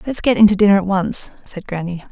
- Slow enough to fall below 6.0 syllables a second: No, 6.1 syllables/s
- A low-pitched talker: No, high, 195 Hz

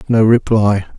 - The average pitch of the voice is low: Yes, low, 110 Hz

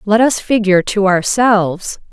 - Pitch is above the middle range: Yes, high, 205 Hz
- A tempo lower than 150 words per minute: Yes, average, 140 wpm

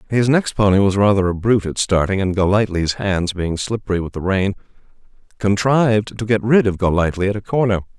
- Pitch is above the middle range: No, low, 100 Hz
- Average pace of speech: Yes, average, 195 wpm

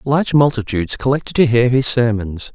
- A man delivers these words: Yes, male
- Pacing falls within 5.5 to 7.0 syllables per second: Yes, 5.7 syllables/s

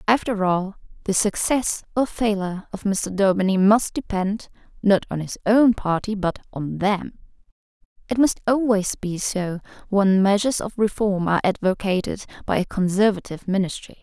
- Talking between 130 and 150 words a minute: Yes, average, 145 wpm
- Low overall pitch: No, high, 200 Hz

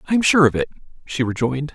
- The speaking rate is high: Yes, fast, 240 wpm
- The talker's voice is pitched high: No, medium, 145 Hz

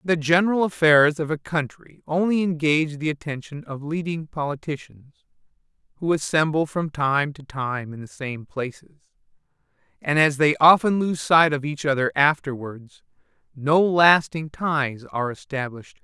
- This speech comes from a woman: No, male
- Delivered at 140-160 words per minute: Yes, average, 150 wpm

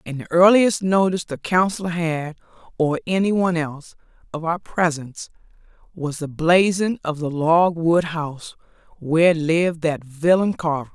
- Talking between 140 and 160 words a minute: Yes, average, 150 wpm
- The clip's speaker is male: No, female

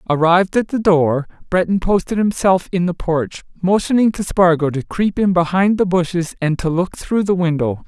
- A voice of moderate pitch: Yes, medium, 180 Hz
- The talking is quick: No, average, 190 wpm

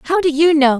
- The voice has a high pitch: Yes, very high, 305 Hz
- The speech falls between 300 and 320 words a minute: Yes, fast, 305 wpm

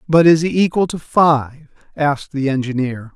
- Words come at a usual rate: Yes, average, 170 wpm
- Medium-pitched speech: Yes, medium, 150 Hz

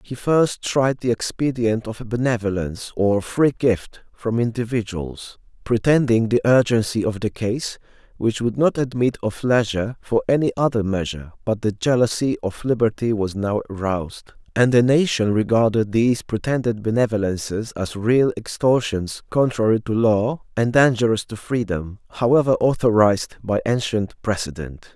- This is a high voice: No, low, 115 Hz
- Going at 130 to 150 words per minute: Yes, average, 140 wpm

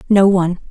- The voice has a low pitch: No, high, 190 Hz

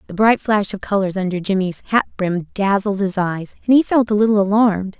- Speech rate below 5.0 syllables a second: No, 5.6 syllables/s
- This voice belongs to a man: No, female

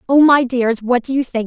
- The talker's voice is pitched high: Yes, very high, 250 Hz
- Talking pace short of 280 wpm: No, fast, 285 wpm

